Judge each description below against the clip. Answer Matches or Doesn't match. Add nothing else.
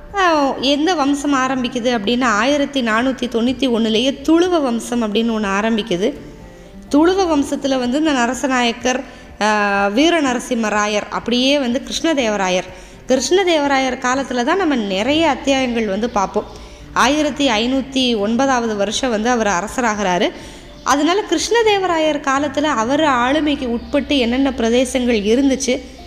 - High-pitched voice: Matches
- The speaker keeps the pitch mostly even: Doesn't match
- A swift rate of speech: Doesn't match